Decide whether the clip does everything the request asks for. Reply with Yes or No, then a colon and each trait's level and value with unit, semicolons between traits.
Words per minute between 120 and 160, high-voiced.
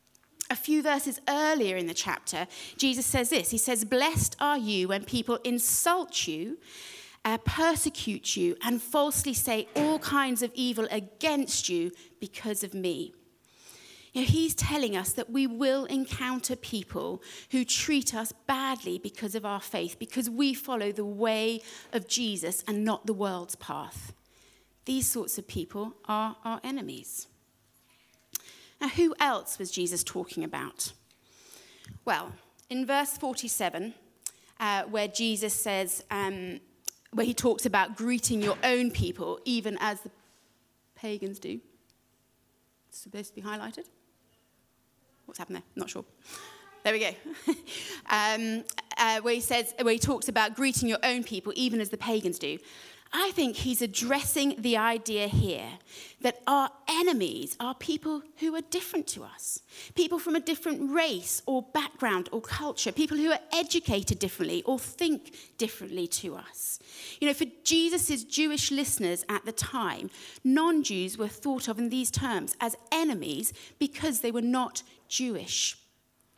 Yes: average, 150 wpm; high, 245 Hz